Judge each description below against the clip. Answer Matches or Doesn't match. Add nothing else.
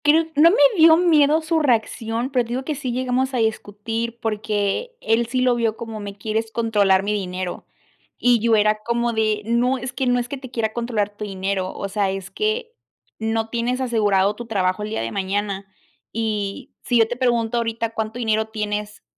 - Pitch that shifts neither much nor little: Matches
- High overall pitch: Matches